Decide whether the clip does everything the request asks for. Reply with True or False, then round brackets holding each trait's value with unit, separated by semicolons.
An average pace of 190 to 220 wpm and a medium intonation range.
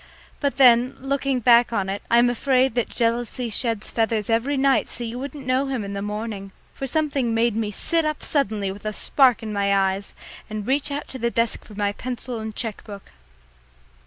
True (205 wpm; 3.8 semitones)